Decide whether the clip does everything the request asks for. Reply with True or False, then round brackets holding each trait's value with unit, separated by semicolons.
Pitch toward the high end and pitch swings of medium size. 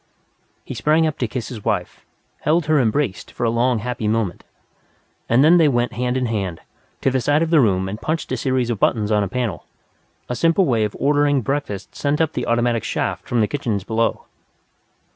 False (125 Hz; 4.6 semitones)